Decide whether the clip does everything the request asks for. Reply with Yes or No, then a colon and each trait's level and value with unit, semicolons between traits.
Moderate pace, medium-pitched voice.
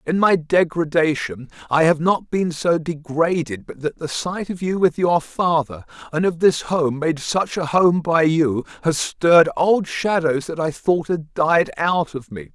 Yes: average, 190 wpm; medium, 160 Hz